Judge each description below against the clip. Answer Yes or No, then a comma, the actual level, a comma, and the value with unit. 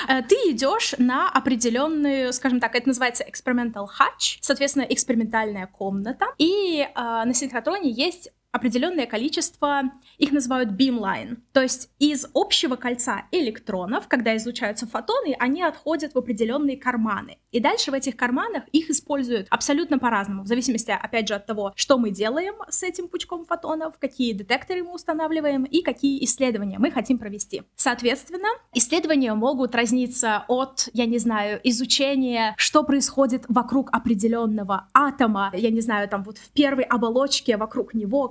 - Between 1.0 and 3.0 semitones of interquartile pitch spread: No, average, 3.6 semitones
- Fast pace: No, average, 145 wpm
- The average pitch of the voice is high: Yes, very high, 255 Hz